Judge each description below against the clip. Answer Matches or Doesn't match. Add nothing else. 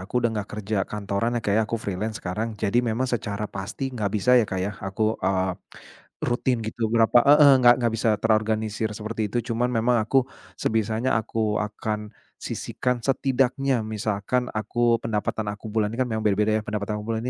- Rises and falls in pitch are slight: Matches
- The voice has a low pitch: Matches